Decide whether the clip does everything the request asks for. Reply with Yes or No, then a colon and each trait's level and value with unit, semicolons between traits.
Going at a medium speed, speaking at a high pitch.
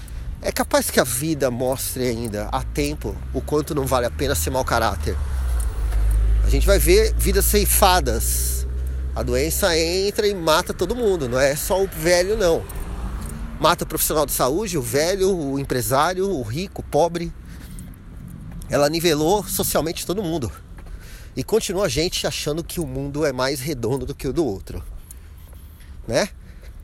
No: average, 160 wpm; low, 135 Hz